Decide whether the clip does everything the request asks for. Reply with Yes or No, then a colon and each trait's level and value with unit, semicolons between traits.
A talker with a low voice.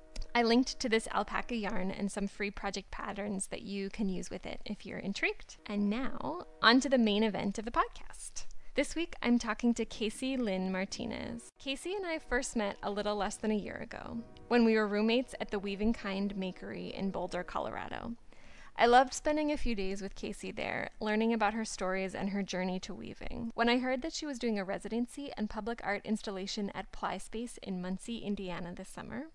No: high, 215 Hz